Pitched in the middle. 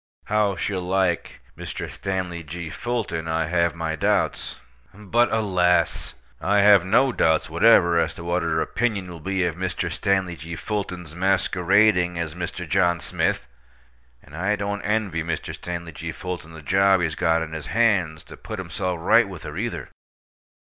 No: very low, 90 Hz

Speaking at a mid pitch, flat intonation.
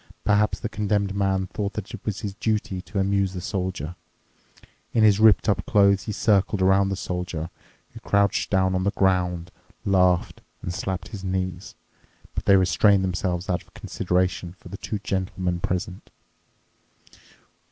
No: very low, 95 Hz; narrow, 1.7 semitones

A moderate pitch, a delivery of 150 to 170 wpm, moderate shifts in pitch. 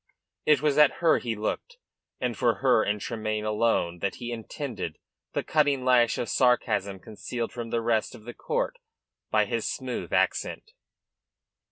No: low, 120 Hz; average, 160 wpm; average, 3.4 semitones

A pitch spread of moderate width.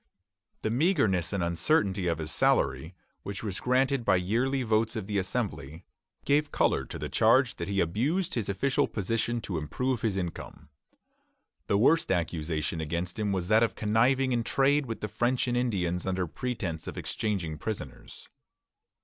No: wide, 5.8 semitones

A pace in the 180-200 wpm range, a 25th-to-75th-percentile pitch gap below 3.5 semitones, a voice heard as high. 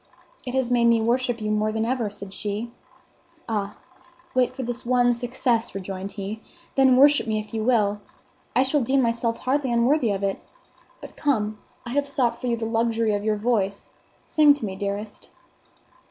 Yes: average, 185 wpm; average, 3.1 semitones; high, 230 Hz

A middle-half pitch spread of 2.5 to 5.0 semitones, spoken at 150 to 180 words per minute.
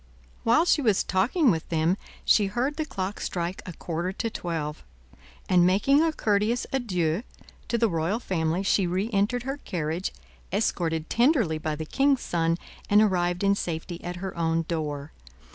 No: wide, 5.4 semitones; average, 160 wpm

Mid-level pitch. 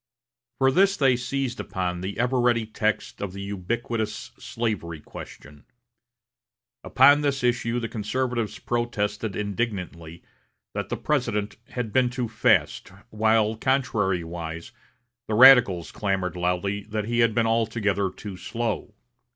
No: low, 110 Hz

